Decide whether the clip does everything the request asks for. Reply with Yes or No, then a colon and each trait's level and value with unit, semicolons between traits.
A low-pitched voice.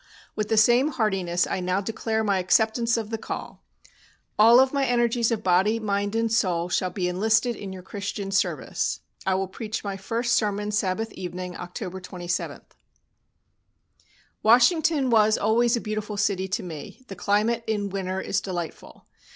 No: high, 210 Hz